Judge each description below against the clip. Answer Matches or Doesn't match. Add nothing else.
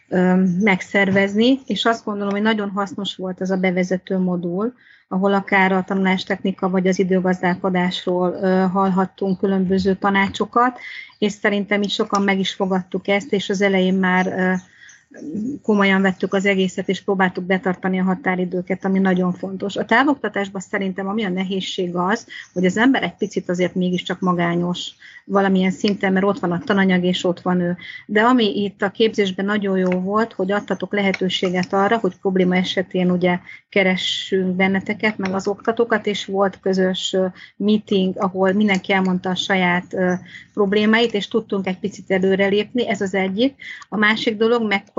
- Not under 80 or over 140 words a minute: Doesn't match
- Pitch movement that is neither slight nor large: Doesn't match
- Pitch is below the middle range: Doesn't match